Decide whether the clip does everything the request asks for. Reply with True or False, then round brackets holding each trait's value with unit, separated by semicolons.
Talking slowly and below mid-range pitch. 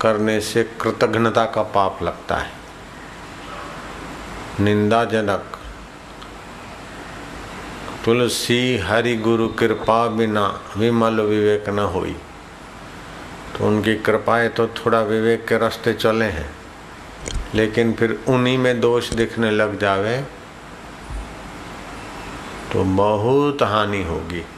True (95 wpm; 110 Hz)